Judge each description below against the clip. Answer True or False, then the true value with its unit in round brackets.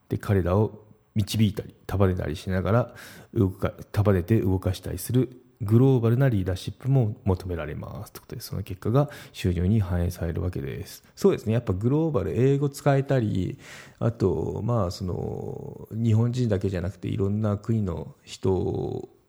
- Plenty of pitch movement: False (4.8 semitones)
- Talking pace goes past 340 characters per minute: False (315 characters per minute)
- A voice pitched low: True (110 Hz)